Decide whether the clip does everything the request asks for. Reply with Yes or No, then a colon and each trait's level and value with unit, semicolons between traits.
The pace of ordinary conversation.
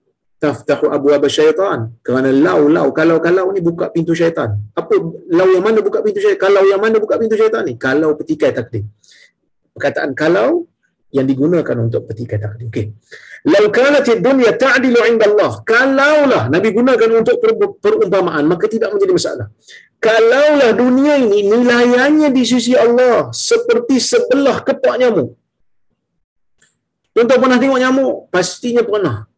No: fast, 145 wpm